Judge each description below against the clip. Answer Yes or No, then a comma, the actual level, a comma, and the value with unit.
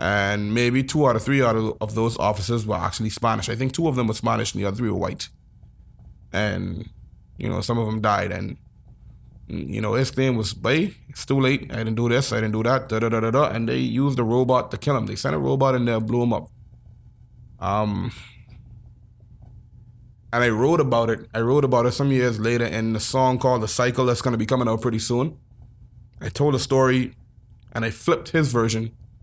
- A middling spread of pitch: No, narrow, 2.2 semitones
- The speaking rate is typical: No, fast, 225 wpm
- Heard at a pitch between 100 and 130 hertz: Yes, low, 115 Hz